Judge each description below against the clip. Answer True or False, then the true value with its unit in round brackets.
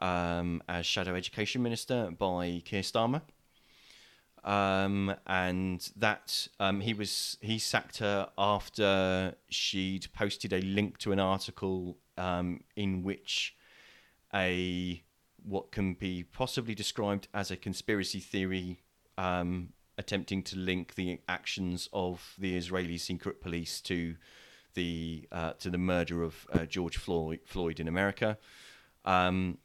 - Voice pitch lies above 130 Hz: False (95 Hz)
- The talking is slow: True (130 wpm)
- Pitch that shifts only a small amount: True (2.2 semitones)